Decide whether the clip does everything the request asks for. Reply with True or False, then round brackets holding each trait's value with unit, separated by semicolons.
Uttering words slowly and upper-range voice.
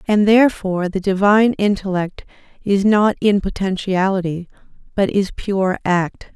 True (125 wpm; 195 Hz)